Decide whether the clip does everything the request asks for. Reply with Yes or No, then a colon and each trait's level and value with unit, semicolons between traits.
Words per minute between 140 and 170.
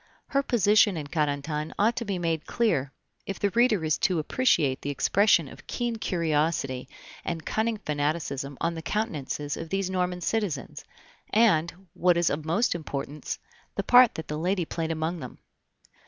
Yes: average, 165 wpm